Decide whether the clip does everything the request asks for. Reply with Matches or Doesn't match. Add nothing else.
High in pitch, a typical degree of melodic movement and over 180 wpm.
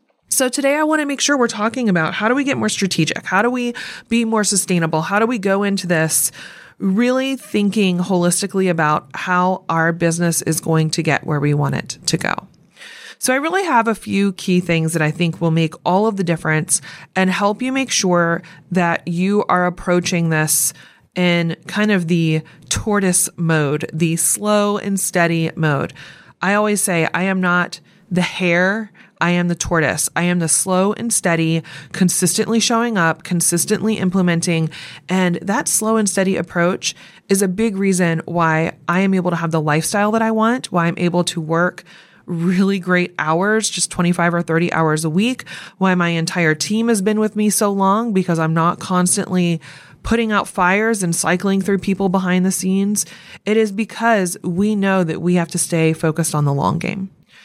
Doesn't match